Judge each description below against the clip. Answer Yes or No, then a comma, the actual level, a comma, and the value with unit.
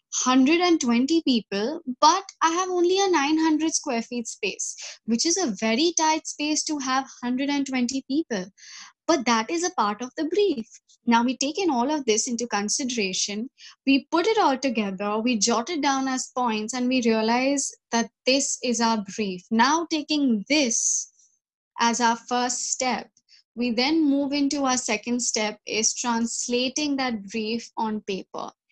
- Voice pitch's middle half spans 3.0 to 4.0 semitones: No, average, 4.9 semitones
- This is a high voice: Yes, very high, 255 Hz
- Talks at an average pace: Yes, average, 165 wpm